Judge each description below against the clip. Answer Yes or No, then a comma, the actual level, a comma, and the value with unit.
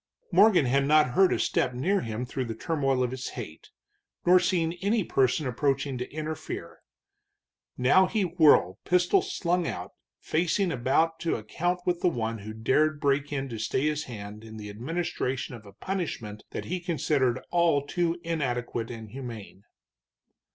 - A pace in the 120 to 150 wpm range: No, average, 165 wpm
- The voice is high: No, medium, 140 Hz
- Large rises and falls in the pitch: Yes, wide, 6.1 semitones